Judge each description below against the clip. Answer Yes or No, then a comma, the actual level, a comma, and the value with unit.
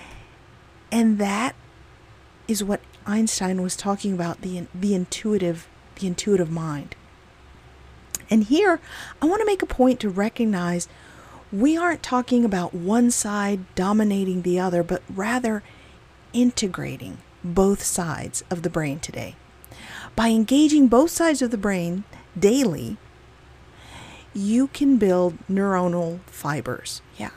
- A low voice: No, high, 200 Hz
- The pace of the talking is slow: Yes, slow, 125 wpm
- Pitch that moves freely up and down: No, average, 4.7 semitones